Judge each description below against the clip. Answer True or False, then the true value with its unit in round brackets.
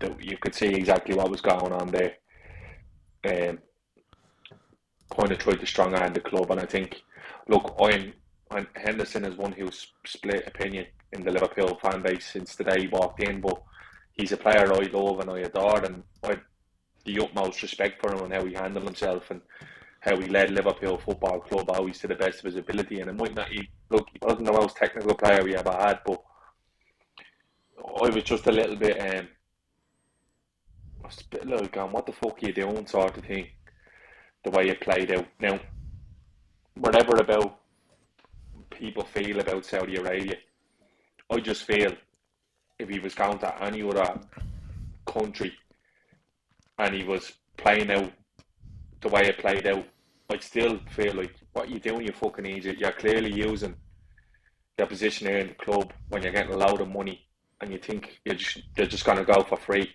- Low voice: True (95 Hz)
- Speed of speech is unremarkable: True (180 wpm)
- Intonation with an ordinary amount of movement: False (1.5 semitones)